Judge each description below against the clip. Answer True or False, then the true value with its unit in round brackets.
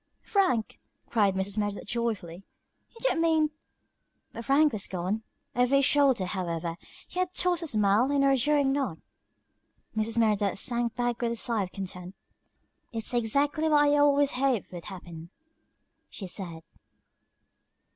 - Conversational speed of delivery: True (150 wpm)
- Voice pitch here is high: True (235 Hz)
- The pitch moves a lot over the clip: True (6.3 semitones)